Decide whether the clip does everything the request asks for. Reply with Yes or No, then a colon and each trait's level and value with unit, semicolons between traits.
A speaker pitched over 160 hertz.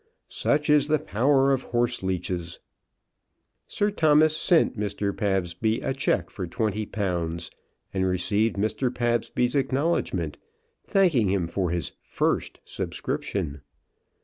No: low, 110 Hz